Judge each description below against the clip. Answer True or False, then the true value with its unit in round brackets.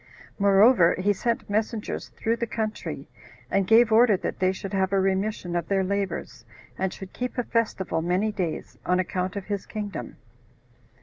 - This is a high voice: True (195 Hz)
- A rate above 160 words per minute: True (170 wpm)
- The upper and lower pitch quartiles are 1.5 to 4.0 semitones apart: True (2.7 semitones)